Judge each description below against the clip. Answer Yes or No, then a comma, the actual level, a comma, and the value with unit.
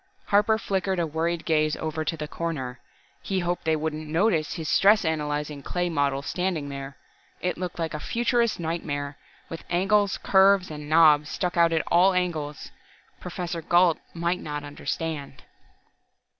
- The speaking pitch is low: No, medium, 165 Hz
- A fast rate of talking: No, average, 155 wpm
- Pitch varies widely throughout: No, average, 3.2 semitones